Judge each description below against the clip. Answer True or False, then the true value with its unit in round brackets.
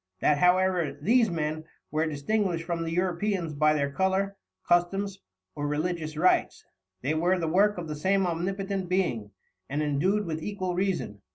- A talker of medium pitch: True (175 Hz)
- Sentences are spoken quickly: False (160 wpm)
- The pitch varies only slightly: False (3.8 semitones)